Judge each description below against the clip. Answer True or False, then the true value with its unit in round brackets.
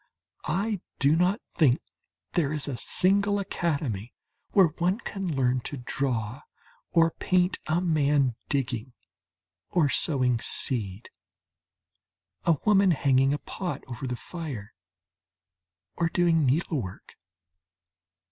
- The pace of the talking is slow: True (110 wpm)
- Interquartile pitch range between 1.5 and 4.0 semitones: False (5.4 semitones)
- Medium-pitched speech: True (150 Hz)